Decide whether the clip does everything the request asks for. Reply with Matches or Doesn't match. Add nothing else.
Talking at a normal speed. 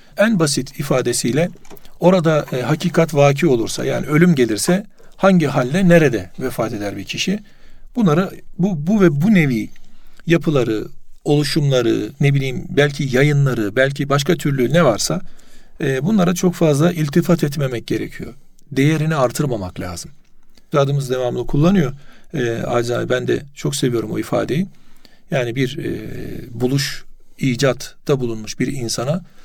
Matches